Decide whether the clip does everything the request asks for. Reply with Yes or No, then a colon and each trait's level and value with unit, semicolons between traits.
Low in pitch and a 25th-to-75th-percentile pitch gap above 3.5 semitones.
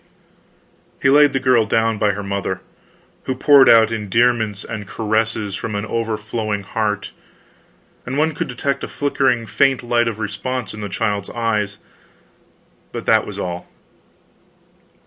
No: low, 110 Hz; average, 3.1 semitones